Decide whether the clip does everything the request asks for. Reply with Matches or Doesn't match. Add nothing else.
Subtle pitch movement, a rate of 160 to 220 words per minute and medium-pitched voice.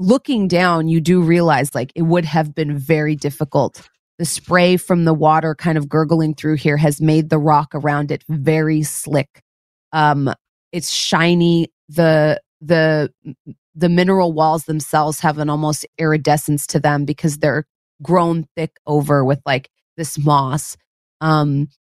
Doesn't match